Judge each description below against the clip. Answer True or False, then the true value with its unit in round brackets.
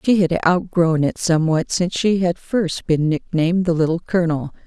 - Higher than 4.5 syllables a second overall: True (5.3 syllables/s)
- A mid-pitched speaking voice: True (170 Hz)